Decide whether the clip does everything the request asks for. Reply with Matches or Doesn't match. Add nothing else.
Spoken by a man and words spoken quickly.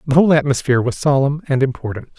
Doesn't match